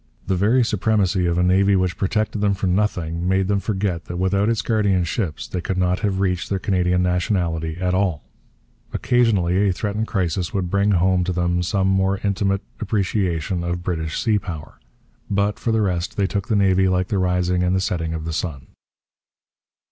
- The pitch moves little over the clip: Yes, narrow, 2.2 semitones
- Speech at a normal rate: Yes, average, 190 wpm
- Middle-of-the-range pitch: No, very low, 95 Hz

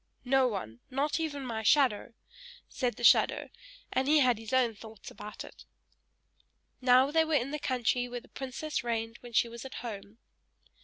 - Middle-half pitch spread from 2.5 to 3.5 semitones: Yes, average, 3.0 semitones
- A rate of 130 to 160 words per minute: No, average, 175 wpm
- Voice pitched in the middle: No, high, 245 Hz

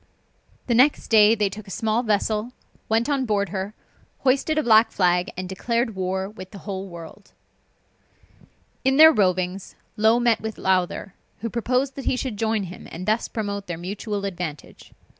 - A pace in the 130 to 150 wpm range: No, average, 170 wpm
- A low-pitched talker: No, high, 210 Hz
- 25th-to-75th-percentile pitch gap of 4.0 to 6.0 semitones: No, average, 3.6 semitones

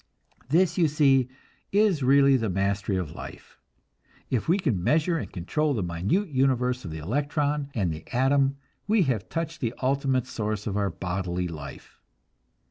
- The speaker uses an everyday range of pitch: No, wide, 7.0 semitones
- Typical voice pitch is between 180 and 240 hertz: No, low, 130 Hz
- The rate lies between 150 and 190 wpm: Yes, average, 160 wpm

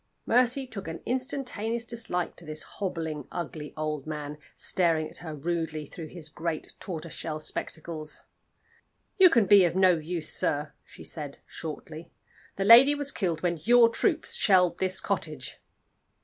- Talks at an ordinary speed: Yes, average, 150 wpm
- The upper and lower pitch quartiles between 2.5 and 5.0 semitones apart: No, wide, 5.5 semitones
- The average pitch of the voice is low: No, medium, 170 Hz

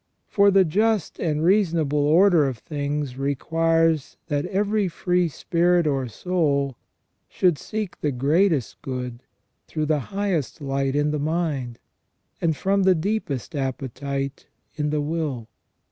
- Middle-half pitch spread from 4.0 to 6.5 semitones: Yes, average, 4.3 semitones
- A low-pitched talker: No, medium, 155 Hz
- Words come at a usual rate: No, slow, 130 wpm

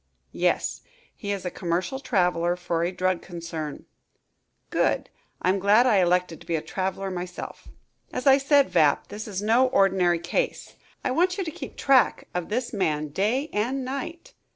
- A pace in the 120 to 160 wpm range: No, average, 170 wpm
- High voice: Yes, high, 195 Hz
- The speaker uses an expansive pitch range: Yes, wide, 6.5 semitones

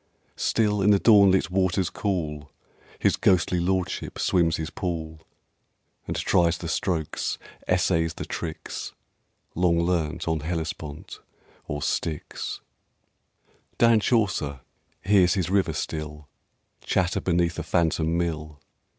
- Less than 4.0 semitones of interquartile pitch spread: Yes, average, 2.9 semitones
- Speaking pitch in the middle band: No, very low, 85 Hz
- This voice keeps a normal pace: No, slow, 115 wpm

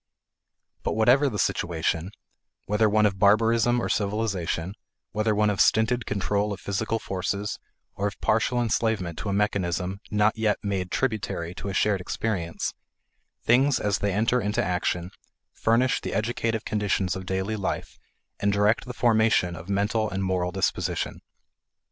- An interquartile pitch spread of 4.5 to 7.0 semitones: No, average, 2.8 semitones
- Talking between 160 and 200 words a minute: No, average, 150 wpm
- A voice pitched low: Yes, low, 105 Hz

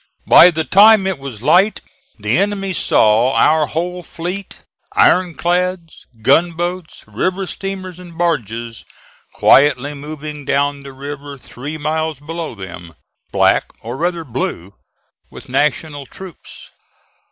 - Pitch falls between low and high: Yes, medium, 155 Hz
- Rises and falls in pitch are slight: No, average, 4.5 semitones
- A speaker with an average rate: No, slow, 120 wpm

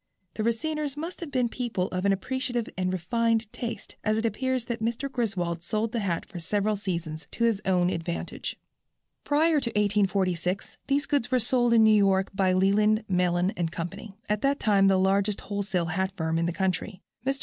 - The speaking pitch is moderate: No, high, 205 Hz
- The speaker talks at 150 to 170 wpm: No, average, 190 wpm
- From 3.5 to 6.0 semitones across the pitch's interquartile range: Yes, average, 4.2 semitones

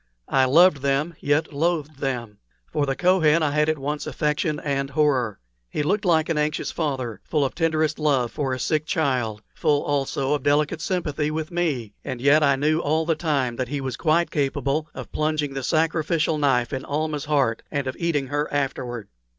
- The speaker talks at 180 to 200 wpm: Yes, average, 190 wpm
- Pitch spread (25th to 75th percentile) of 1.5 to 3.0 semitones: Yes, narrow, 2.5 semitones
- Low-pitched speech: No, medium, 145 Hz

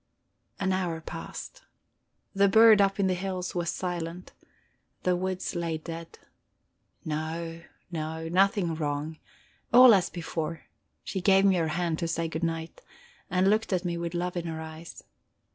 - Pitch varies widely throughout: No, narrow, 2.5 semitones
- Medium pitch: Yes, medium, 175 Hz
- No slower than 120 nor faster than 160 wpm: Yes, average, 155 wpm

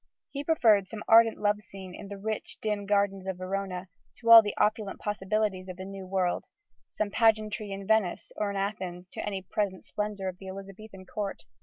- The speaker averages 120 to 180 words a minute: No, average, 190 wpm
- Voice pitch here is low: No, high, 200 Hz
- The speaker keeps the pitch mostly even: Yes, narrow, 1.9 semitones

